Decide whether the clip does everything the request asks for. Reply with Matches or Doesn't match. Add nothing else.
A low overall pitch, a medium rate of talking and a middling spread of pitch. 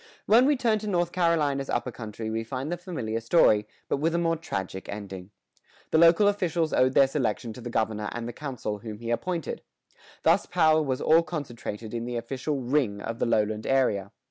Doesn't match